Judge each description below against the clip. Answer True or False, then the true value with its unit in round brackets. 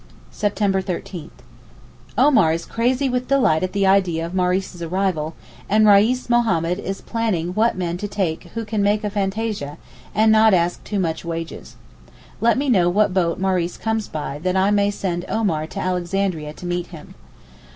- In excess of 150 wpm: True (165 wpm)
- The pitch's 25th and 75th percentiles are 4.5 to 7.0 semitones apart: False (4.0 semitones)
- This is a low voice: False (190 Hz)